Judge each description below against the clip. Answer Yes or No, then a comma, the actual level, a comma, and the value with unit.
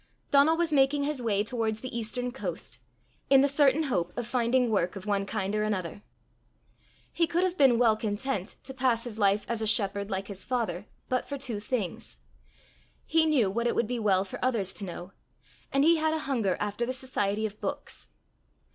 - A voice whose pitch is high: Yes, high, 230 Hz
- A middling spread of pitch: Yes, average, 4.6 semitones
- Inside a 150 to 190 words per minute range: No, average, 200 wpm